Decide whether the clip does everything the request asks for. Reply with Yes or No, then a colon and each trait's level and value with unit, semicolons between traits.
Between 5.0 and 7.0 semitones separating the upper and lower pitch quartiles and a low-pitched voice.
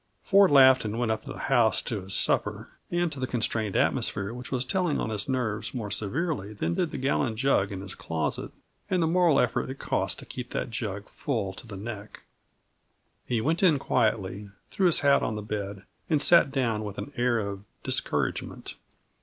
Yes: average, 5.3 semitones; low, 120 Hz